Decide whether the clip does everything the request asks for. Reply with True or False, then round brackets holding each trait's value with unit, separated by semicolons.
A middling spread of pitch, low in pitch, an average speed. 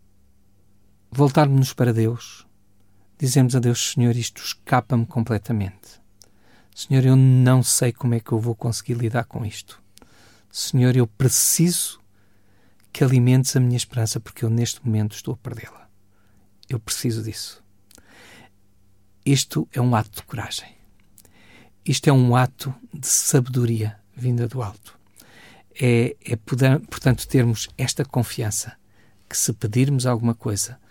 True (3.8 semitones; 120 Hz; 130 wpm)